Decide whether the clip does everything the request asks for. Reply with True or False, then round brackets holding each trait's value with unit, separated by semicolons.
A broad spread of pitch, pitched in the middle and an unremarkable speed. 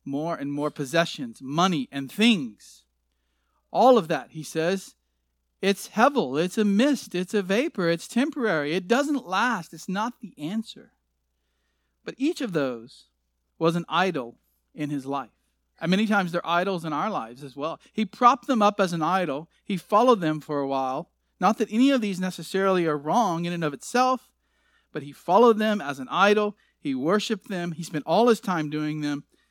True (7.1 semitones; 175 Hz; 185 wpm)